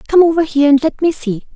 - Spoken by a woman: Yes, female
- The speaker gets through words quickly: Yes, fast, 270 wpm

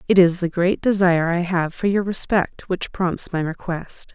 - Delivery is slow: No, fast, 205 wpm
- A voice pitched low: No, medium, 180 Hz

